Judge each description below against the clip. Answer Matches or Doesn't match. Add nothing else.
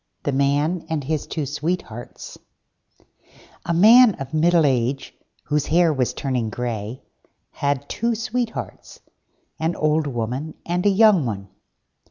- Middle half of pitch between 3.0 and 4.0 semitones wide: Doesn't match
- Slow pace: Matches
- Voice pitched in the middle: Matches